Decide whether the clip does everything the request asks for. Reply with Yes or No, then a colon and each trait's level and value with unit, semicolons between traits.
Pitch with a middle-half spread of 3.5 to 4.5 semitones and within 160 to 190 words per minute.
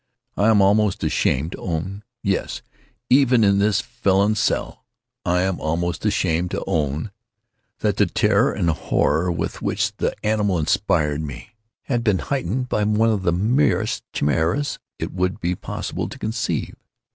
No: average, 4.0 semitones; average, 145 wpm